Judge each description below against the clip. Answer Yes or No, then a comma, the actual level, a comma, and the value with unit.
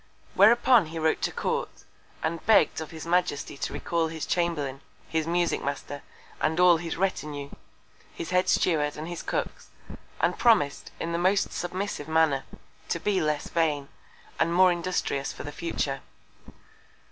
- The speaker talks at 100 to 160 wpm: Yes, average, 155 wpm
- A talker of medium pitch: Yes, medium, 165 Hz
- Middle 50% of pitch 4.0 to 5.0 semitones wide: No, average, 3.1 semitones